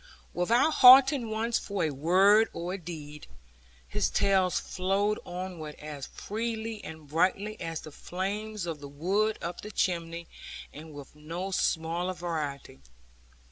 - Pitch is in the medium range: Yes, medium, 180 Hz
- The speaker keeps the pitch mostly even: No, average, 4.7 semitones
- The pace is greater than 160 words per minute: No, average, 140 wpm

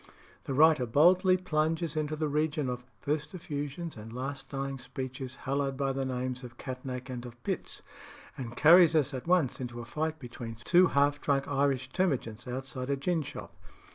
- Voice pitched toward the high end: No, low, 135 Hz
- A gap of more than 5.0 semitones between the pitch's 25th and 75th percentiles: No, average, 3.4 semitones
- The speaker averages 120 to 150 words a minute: No, average, 175 wpm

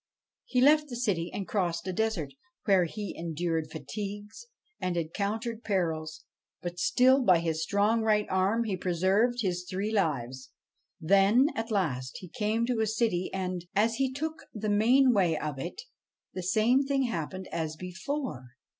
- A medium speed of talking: Yes, average, 160 wpm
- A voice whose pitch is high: Yes, high, 195 Hz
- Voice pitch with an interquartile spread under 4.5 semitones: No, average, 5.0 semitones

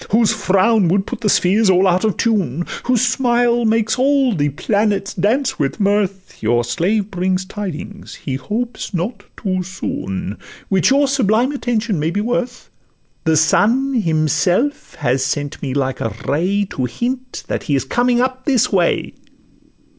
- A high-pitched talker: Yes, high, 200 Hz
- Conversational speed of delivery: Yes, average, 155 wpm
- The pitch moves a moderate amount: No, wide, 6.0 semitones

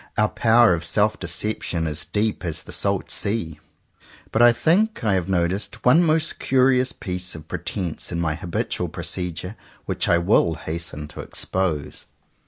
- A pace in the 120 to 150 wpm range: No, average, 160 wpm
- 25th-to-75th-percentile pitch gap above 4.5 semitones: Yes, average, 5.3 semitones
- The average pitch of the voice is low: Yes, very low, 95 Hz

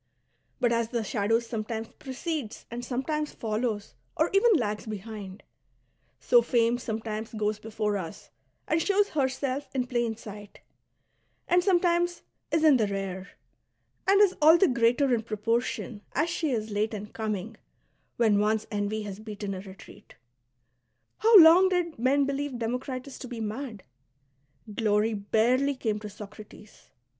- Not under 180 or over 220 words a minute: No, average, 150 wpm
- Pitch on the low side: No, high, 230 Hz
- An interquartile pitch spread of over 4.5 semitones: Yes, average, 4.9 semitones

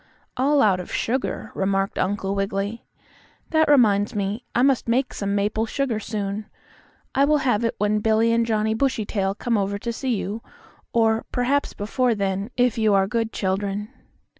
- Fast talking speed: No, average, 165 wpm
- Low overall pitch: No, high, 220 Hz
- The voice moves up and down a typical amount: Yes, average, 3.3 semitones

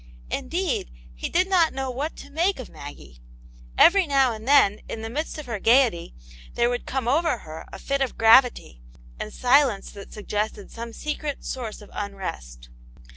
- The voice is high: Yes, high, 245 Hz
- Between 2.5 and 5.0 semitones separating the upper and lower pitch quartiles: No, wide, 5.4 semitones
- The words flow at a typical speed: Yes, average, 175 wpm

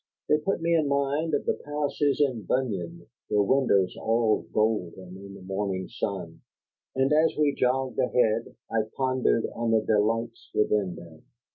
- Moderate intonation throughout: No, wide, 5.7 semitones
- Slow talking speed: No, average, 155 wpm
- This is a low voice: Yes, low, 115 Hz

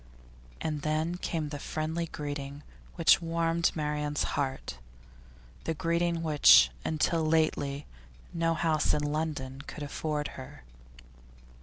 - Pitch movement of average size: No, narrow, 2.2 semitones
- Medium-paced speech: No, slow, 115 wpm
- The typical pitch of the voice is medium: Yes, medium, 155 Hz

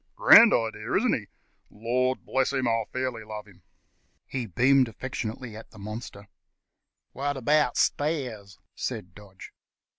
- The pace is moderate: No, slow, 130 wpm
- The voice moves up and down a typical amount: Yes, average, 3.8 semitones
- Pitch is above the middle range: No, low, 120 Hz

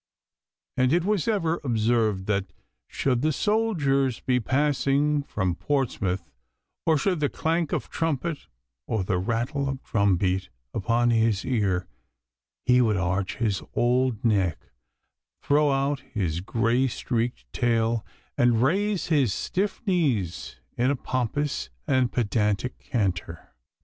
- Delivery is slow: Yes, slow, 130 wpm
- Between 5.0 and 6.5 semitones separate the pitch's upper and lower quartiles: Yes, wide, 5.6 semitones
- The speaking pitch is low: Yes, low, 125 Hz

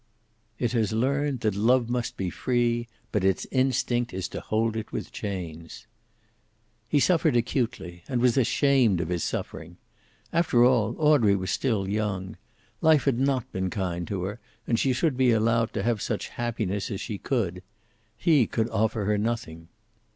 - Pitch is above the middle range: No, low, 115 Hz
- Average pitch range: Yes, average, 4.3 semitones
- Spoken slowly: No, average, 165 wpm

